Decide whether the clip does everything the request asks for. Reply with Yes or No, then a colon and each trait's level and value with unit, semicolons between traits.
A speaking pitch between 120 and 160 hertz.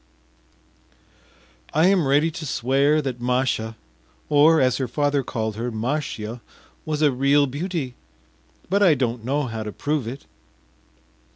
Yes: low, 135 Hz